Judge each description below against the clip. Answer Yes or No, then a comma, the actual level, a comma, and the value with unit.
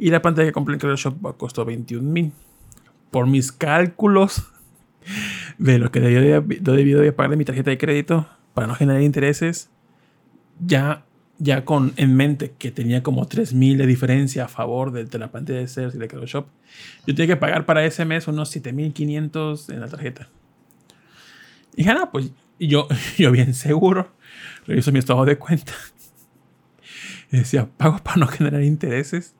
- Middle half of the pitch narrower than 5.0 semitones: Yes, average, 3.3 semitones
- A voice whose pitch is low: No, medium, 145 Hz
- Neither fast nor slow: Yes, average, 165 wpm